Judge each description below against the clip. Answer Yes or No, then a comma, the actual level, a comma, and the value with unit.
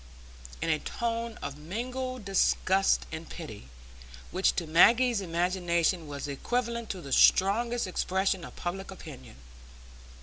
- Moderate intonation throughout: No, wide, 5.8 semitones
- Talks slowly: Yes, slow, 125 wpm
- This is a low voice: No, high, 190 Hz